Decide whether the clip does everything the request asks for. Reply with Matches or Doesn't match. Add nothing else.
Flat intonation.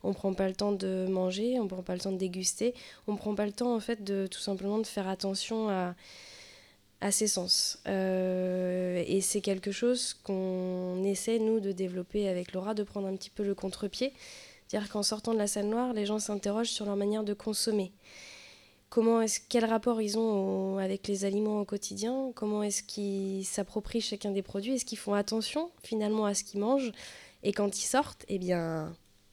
Matches